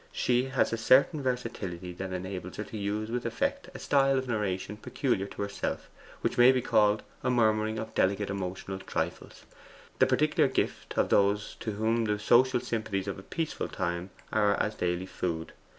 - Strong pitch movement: No, average, 4.0 semitones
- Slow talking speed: No, average, 180 wpm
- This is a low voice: Yes, low, 105 Hz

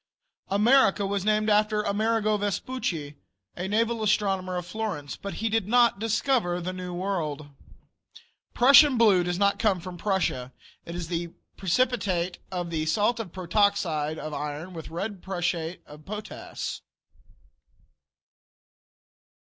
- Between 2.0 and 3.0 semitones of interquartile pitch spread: No, average, 3.8 semitones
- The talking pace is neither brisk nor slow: No, slow, 130 wpm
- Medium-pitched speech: No, high, 195 Hz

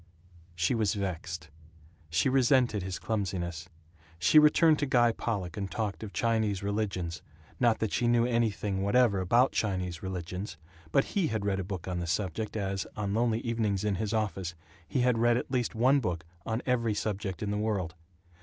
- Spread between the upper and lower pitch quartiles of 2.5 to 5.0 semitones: Yes, average, 3.9 semitones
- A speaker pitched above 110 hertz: No, low, 105 Hz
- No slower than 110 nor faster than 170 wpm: No, average, 180 wpm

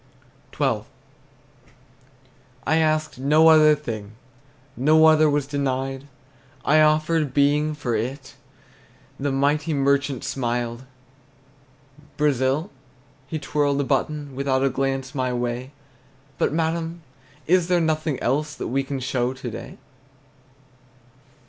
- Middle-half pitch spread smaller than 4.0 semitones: Yes, average, 2.7 semitones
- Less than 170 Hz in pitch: Yes, medium, 140 Hz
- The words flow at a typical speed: No, slow, 115 wpm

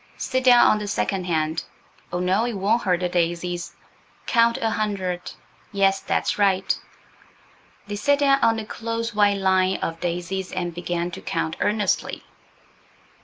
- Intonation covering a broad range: No, average, 3.9 semitones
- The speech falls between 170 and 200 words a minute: No, average, 145 wpm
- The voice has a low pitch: No, high, 195 Hz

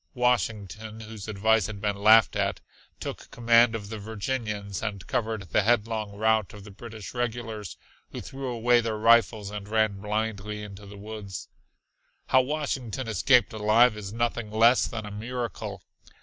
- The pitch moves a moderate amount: No, narrow, 2.2 semitones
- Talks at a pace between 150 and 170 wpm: Yes, average, 155 wpm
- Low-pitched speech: Yes, low, 110 Hz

